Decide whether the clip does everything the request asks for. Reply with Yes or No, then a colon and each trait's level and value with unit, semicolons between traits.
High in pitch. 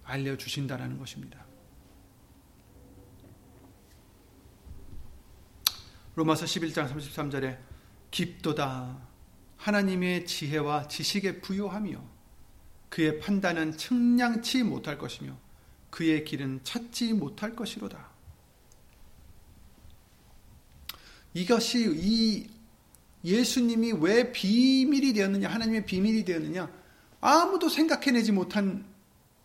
No: medium, 175 Hz